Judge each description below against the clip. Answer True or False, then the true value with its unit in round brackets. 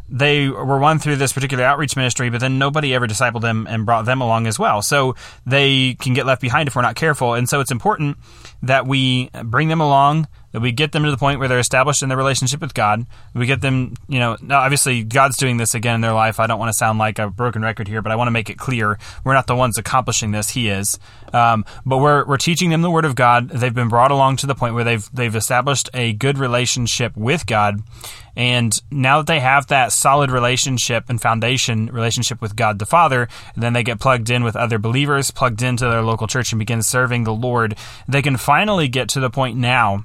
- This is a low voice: True (125 Hz)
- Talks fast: True (240 wpm)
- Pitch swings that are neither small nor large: True (3.0 semitones)